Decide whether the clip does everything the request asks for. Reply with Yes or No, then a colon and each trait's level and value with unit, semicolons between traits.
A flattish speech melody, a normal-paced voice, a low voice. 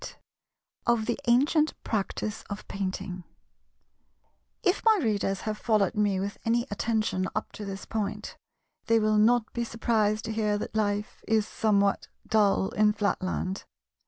No: narrow, 2.0 semitones; average, 150 wpm; high, 215 Hz